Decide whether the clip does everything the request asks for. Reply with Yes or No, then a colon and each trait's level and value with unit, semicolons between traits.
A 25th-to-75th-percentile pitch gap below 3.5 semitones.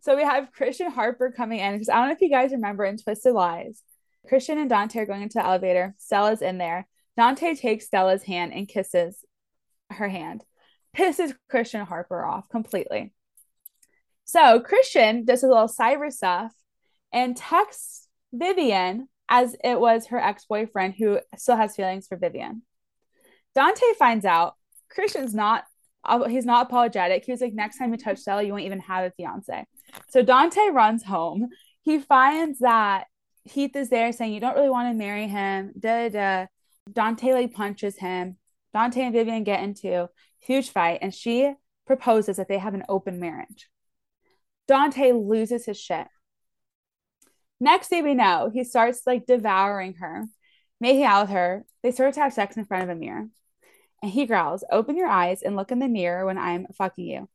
No: average, 4.9 semitones